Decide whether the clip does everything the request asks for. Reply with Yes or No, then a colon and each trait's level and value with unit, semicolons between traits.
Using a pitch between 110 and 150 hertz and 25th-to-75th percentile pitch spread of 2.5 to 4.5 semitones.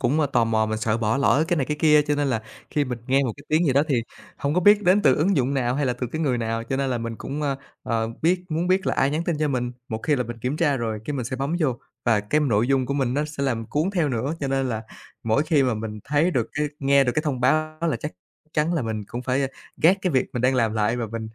Yes: low, 135 Hz; average, 4.2 semitones